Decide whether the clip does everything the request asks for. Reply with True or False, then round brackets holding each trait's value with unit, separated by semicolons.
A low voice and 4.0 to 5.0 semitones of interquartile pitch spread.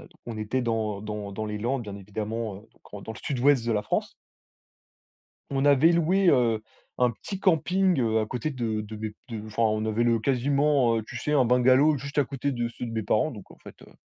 True (120 Hz; 4.3 semitones)